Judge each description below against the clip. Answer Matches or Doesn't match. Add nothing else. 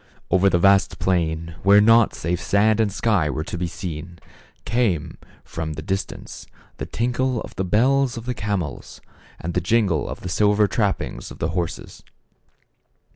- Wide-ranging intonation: Doesn't match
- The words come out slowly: Doesn't match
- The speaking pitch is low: Matches